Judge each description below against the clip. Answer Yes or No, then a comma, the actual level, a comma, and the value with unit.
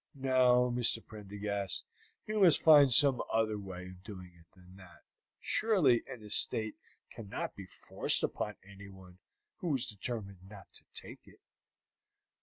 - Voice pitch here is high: No, low, 105 Hz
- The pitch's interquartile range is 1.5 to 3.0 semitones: No, average, 4.5 semitones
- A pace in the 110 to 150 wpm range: Yes, average, 140 wpm